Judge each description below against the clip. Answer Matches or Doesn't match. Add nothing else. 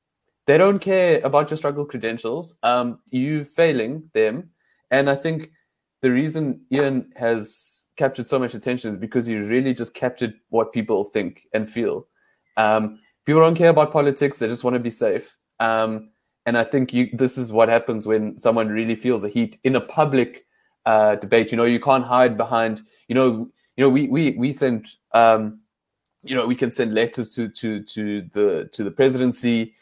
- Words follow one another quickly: Doesn't match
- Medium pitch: Doesn't match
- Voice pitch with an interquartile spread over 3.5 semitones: Doesn't match